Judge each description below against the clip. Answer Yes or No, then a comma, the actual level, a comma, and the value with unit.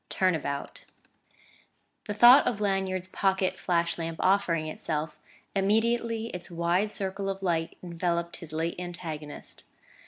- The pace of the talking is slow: Yes, slow, 130 wpm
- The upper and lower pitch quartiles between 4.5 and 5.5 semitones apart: No, average, 2.9 semitones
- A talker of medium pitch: Yes, medium, 180 Hz